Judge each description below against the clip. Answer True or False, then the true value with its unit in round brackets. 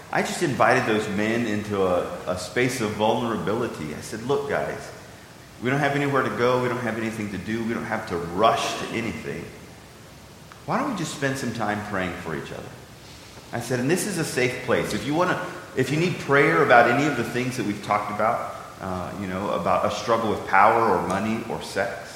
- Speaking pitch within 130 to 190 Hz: False (115 Hz)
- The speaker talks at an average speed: False (220 wpm)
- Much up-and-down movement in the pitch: False (4.8 semitones)